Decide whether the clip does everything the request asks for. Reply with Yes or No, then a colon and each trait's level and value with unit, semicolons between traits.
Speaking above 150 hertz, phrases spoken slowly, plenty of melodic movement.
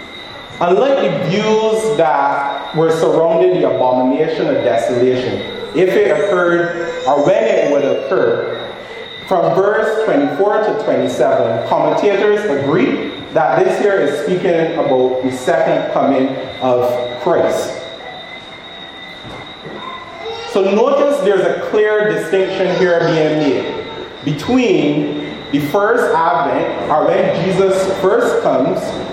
Yes: medium, 185 Hz; slow, 110 wpm; wide, 6.7 semitones